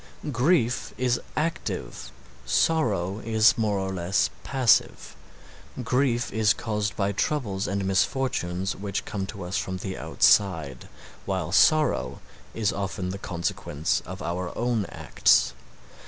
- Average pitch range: Yes, average, 4.2 semitones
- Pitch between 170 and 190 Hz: No, low, 100 Hz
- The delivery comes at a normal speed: No, slow, 125 wpm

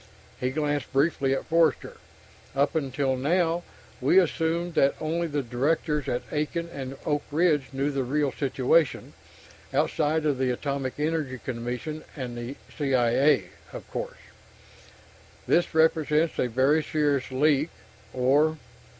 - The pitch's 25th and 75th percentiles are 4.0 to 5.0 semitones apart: No, average, 3.3 semitones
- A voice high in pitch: No, medium, 145 Hz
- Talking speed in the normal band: No, slow, 125 wpm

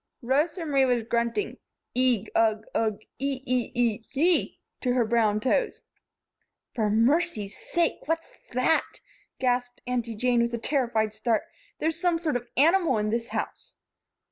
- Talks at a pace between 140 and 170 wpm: Yes, average, 160 wpm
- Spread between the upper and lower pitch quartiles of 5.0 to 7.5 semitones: No, average, 4.4 semitones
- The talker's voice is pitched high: Yes, high, 245 Hz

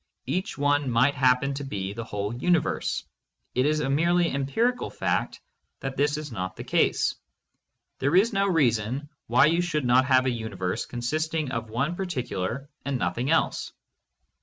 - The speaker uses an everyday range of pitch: Yes, average, 4.6 semitones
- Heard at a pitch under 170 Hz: Yes, low, 135 Hz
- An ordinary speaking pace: Yes, average, 165 wpm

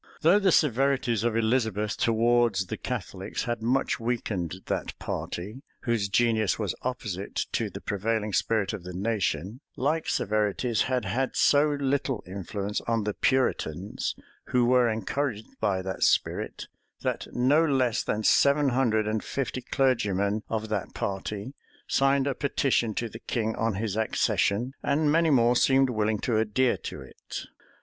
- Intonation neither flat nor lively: Yes, average, 3.9 semitones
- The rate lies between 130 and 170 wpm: Yes, average, 150 wpm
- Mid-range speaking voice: No, low, 115 Hz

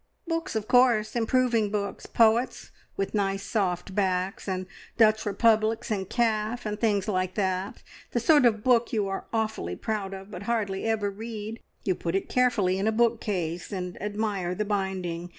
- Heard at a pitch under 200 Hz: No, high, 210 Hz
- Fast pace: No, average, 170 wpm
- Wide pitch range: No, average, 2.8 semitones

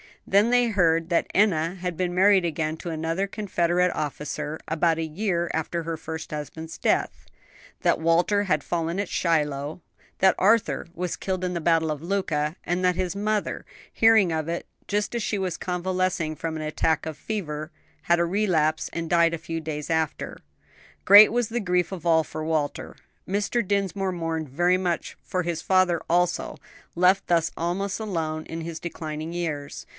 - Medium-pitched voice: Yes, medium, 170 Hz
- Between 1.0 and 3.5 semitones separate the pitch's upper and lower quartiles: Yes, average, 2.8 semitones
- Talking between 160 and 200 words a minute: Yes, average, 175 wpm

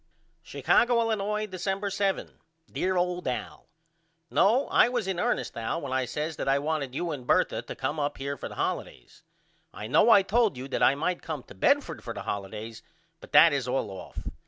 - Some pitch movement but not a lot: No, wide, 7.0 semitones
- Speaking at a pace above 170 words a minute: Yes, average, 200 wpm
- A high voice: No, medium, 160 Hz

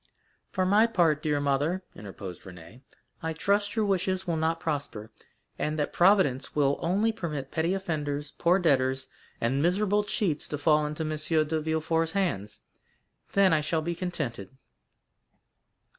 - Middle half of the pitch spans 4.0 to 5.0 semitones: Yes, average, 4.4 semitones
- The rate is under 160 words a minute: Yes, average, 145 wpm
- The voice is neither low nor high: Yes, medium, 160 Hz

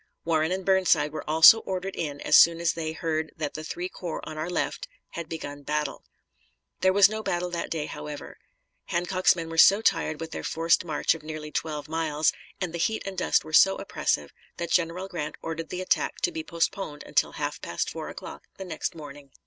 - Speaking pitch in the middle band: Yes, medium, 165 Hz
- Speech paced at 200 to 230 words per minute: Yes, fast, 205 wpm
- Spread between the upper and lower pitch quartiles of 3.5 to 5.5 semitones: No, average, 2.8 semitones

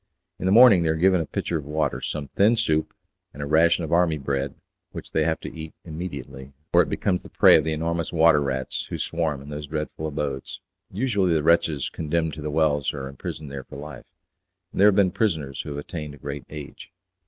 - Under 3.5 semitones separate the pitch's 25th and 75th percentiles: Yes, average, 2.8 semitones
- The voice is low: Yes, very low, 80 Hz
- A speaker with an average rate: No, fast, 220 wpm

